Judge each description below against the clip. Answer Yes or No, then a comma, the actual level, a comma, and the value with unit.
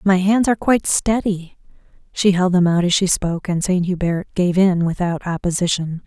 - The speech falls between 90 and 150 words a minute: No, average, 190 wpm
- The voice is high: No, medium, 180 Hz